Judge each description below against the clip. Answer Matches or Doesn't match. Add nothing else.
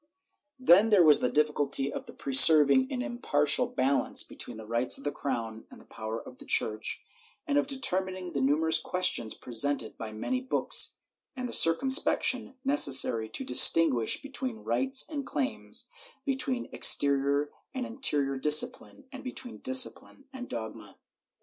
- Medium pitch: Matches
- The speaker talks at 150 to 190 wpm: Matches